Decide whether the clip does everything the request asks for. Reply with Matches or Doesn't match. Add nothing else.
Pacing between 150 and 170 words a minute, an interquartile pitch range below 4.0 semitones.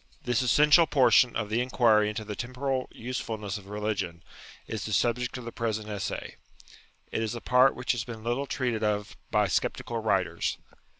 Doesn't match